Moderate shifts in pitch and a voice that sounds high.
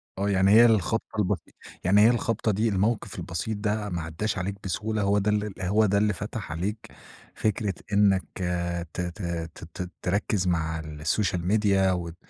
No: average, 3.2 semitones; low, 100 Hz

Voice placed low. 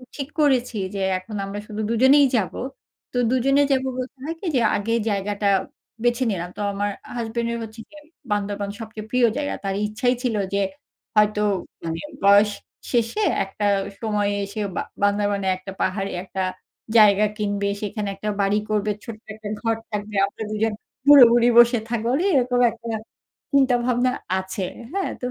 No: high, 215 Hz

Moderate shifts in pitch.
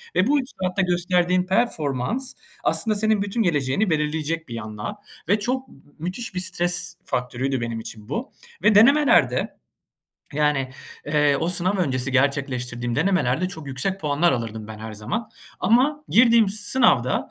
No: wide, 7.9 semitones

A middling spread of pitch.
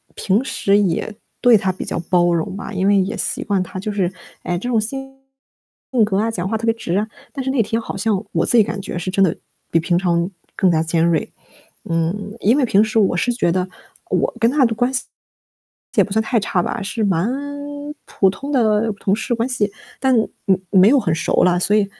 Yes: average, 3.6 semitones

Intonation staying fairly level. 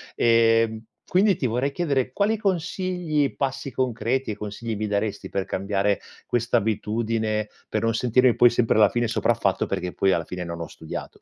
No: average, 4.1 semitones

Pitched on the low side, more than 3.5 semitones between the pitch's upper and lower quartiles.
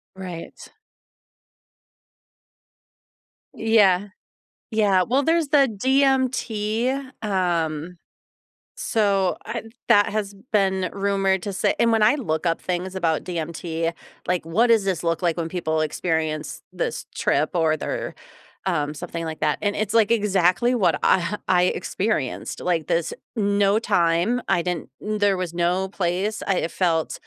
No: high, 190 Hz; average, 4.0 semitones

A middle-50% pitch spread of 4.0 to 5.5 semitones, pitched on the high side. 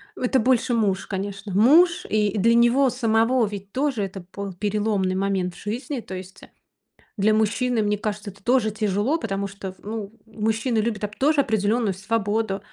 No: average, 2.9 semitones; high, 215 Hz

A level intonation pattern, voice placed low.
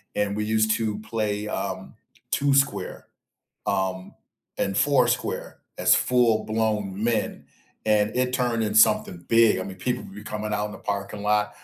Yes: narrow, 1.8 semitones; low, 105 Hz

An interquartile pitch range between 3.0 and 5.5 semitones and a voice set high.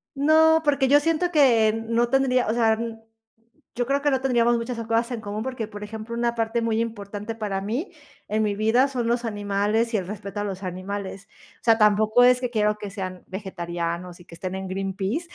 Yes: average, 3.4 semitones; high, 220 Hz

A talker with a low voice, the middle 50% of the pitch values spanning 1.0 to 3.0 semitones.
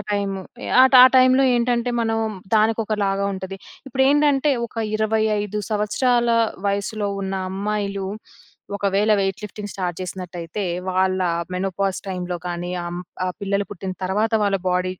No: high, 200 Hz; average, 2.7 semitones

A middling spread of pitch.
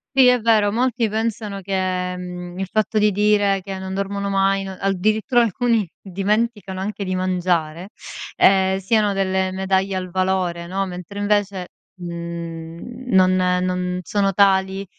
No: narrow, 2.0 semitones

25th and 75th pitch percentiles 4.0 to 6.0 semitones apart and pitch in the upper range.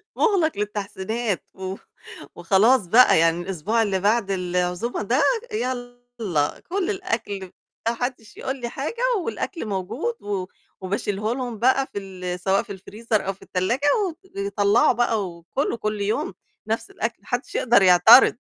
Yes: average, 4.3 semitones; high, 215 Hz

